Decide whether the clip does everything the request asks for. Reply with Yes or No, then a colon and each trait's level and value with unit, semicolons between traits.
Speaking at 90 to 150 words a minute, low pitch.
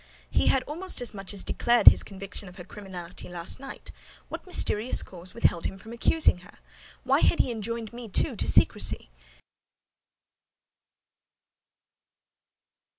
No: average, 140 wpm; high, 205 Hz